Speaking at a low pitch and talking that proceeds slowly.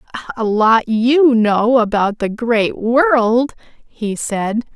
No: high, 230 Hz; slow, 125 wpm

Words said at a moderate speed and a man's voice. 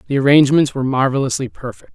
Yes: average, 155 wpm; male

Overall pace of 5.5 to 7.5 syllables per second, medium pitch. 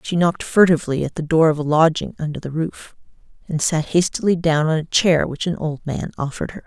Yes: 5.9 syllables/s; medium, 160 Hz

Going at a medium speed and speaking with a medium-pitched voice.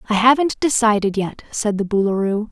No: average, 165 wpm; high, 215 Hz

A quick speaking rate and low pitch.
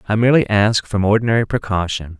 No: average, 165 wpm; low, 105 Hz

